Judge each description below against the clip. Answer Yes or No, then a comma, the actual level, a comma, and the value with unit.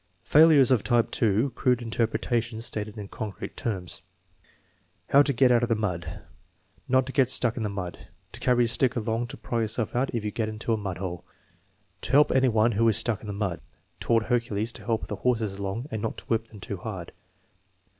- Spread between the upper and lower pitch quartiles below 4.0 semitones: Yes, narrow, 2.5 semitones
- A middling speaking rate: No, fast, 210 wpm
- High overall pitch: No, low, 115 Hz